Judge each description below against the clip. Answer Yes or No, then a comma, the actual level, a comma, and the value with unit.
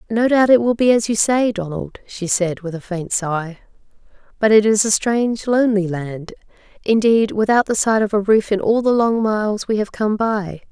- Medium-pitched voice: No, high, 210 Hz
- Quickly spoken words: Yes, fast, 215 wpm